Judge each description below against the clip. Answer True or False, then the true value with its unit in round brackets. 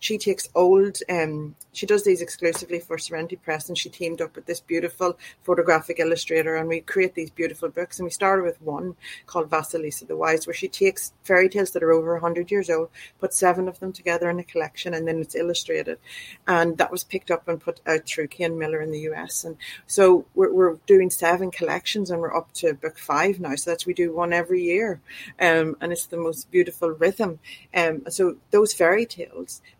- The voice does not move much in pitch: True (2.0 semitones)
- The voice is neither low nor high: True (170 Hz)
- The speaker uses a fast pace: True (210 wpm)